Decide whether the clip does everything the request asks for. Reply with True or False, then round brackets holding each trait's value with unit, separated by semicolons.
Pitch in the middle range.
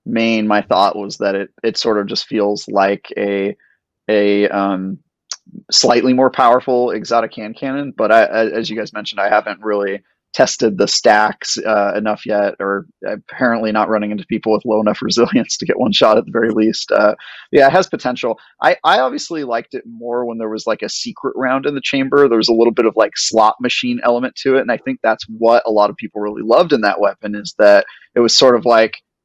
False (110 Hz)